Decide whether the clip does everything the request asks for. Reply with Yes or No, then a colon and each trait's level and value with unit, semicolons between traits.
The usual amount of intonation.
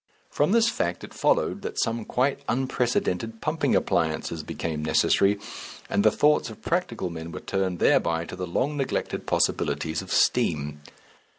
No: wide, 8.2 semitones